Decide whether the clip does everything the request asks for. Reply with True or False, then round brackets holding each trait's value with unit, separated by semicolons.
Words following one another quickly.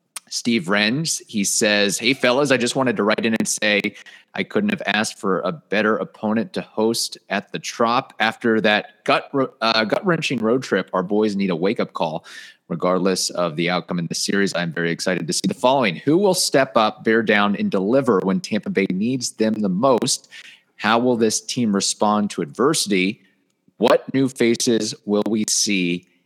False (190 wpm)